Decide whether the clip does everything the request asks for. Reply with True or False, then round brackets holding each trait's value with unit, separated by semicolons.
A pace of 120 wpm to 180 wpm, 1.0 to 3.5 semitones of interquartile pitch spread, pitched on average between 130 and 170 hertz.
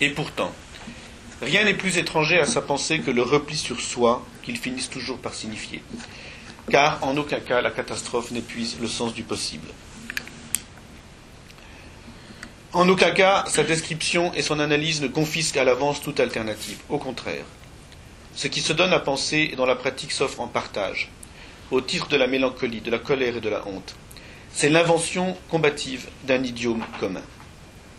False (165 wpm; 4.7 semitones; 140 Hz)